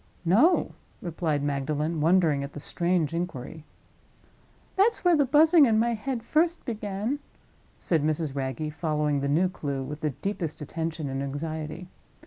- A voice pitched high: No, medium, 165 Hz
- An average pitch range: No, wide, 6.3 semitones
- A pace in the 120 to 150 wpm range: Yes, average, 145 wpm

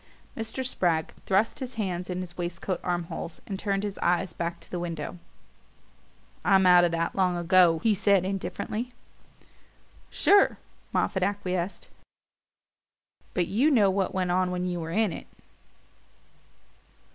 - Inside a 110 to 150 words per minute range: Yes, average, 145 wpm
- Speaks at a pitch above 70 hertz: Yes, medium, 185 Hz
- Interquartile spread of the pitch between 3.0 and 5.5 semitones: No, narrow, 2.4 semitones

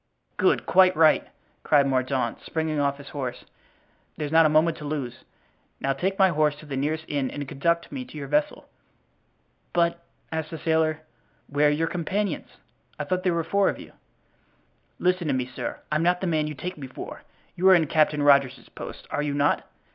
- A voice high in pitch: No, medium, 155 Hz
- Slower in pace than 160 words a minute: No, average, 195 wpm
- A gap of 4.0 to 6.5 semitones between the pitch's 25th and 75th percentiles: No, average, 2.9 semitones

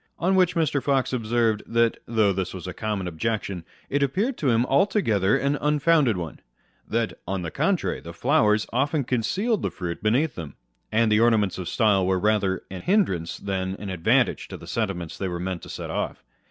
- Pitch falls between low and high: No, low, 110 Hz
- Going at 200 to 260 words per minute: Yes, fast, 205 wpm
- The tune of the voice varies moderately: No, wide, 6.5 semitones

